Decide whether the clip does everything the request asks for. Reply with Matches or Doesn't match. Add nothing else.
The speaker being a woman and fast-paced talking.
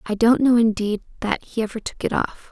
Matches